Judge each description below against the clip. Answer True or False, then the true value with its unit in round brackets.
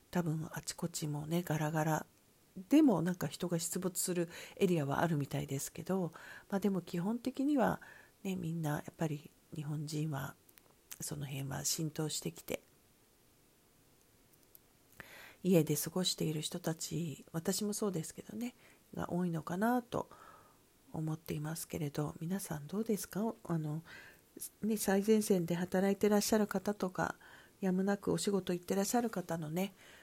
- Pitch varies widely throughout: False (4.0 semitones)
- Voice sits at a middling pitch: True (175 Hz)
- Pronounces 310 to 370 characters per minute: False (295 characters per minute)